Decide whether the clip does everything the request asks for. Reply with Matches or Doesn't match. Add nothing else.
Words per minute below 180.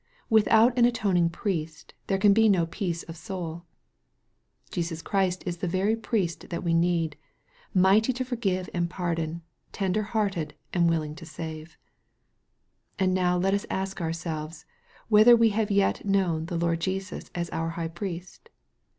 Matches